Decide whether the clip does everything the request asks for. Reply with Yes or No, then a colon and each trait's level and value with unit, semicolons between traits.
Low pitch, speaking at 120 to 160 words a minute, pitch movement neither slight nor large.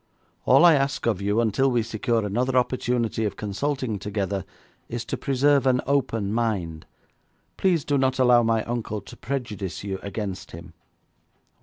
Yes: low, 115 Hz; average, 155 wpm; average, 4.3 semitones